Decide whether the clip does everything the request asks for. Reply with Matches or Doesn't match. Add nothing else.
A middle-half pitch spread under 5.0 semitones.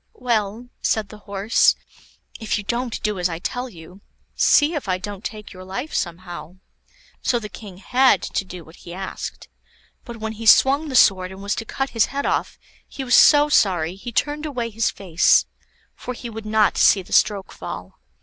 Matches